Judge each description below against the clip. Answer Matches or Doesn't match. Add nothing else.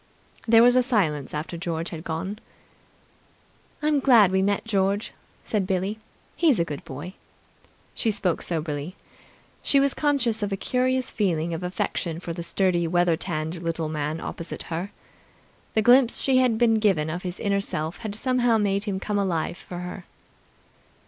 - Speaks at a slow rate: Doesn't match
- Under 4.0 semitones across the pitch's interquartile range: Doesn't match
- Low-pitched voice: Doesn't match